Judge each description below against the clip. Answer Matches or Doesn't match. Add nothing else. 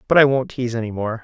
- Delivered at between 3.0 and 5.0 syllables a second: Doesn't match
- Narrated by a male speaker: Matches